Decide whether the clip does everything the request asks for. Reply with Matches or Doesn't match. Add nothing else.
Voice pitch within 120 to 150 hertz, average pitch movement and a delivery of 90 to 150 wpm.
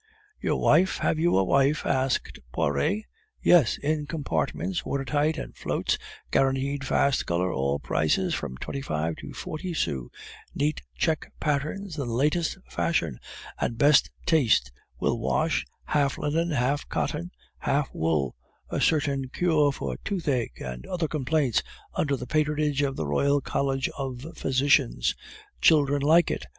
Matches